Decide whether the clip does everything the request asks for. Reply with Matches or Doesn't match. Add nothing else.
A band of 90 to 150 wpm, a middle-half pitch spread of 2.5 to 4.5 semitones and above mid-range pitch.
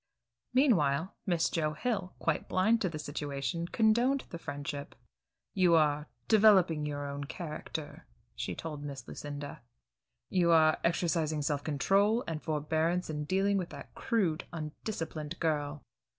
Doesn't match